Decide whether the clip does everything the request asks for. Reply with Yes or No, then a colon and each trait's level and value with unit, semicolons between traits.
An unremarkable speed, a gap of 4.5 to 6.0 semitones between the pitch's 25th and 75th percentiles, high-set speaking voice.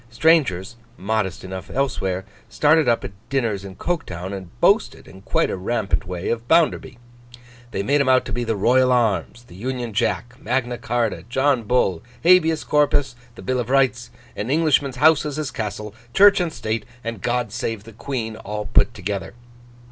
No: average, 175 wpm; average, 4.8 semitones; low, 120 Hz